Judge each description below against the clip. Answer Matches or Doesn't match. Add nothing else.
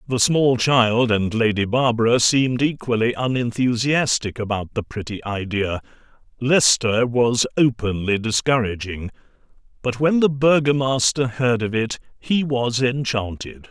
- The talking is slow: Matches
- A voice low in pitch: Matches